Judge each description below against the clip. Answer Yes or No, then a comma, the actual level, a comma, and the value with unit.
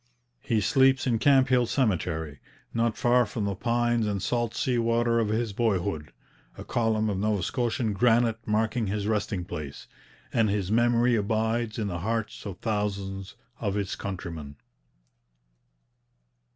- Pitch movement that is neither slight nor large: Yes, average, 3.0 semitones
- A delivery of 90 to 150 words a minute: Yes, average, 140 wpm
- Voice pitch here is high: No, low, 110 Hz